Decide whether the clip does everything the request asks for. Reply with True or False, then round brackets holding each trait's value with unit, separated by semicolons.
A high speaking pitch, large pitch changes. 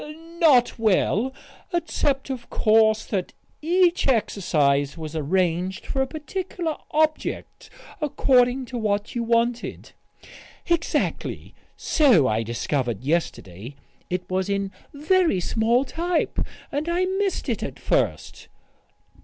True (235 Hz; 8.9 semitones)